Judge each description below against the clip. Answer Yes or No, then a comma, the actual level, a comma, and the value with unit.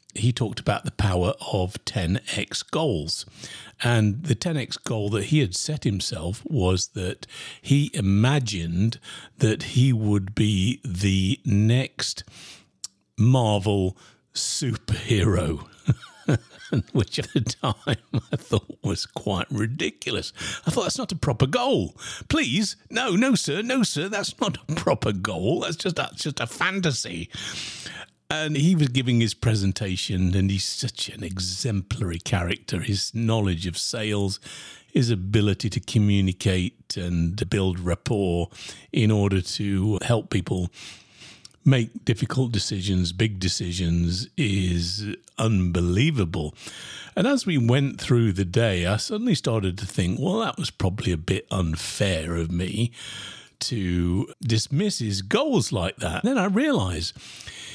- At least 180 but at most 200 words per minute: No, slow, 135 wpm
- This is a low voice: Yes, low, 105 Hz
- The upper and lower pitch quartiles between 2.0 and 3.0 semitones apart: No, average, 4.9 semitones